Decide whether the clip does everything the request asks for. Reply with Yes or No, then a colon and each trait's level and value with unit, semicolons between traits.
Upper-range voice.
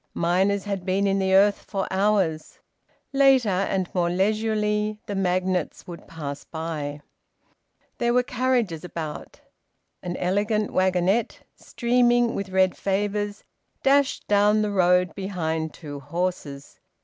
Yes: high, 195 Hz